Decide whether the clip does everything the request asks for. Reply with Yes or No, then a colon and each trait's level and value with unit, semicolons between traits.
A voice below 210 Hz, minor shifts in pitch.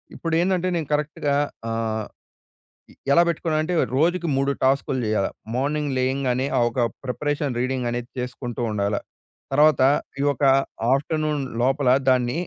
No: low, 135 Hz; average, 3.5 semitones